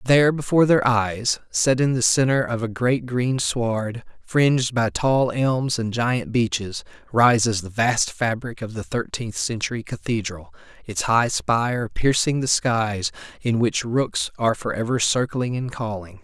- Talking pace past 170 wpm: No, average, 165 wpm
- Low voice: Yes, low, 120 Hz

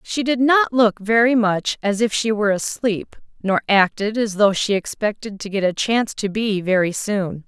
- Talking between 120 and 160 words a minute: No, average, 200 wpm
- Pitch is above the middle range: Yes, high, 210 Hz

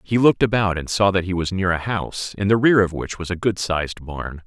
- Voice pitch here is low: Yes, very low, 95 Hz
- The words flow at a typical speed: No, fast, 280 wpm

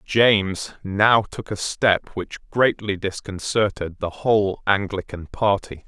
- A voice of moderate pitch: No, low, 100 Hz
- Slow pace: Yes, slow, 120 wpm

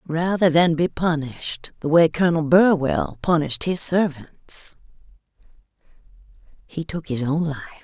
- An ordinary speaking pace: No, slow, 125 wpm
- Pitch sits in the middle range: Yes, medium, 155 Hz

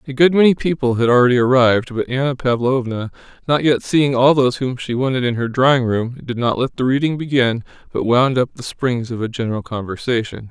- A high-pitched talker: No, low, 125 Hz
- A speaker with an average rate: No, fast, 210 wpm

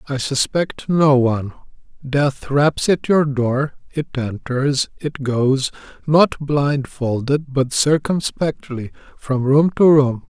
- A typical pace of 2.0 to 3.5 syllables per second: Yes, 3.4 syllables/s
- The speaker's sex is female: No, male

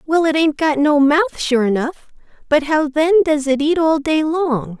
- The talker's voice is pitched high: Yes, very high, 295 Hz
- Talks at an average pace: No, fast, 215 wpm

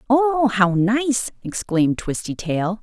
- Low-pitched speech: No, high, 220 Hz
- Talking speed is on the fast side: No, slow, 125 wpm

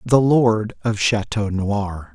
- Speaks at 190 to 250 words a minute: No, average, 140 wpm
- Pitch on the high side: No, low, 110 Hz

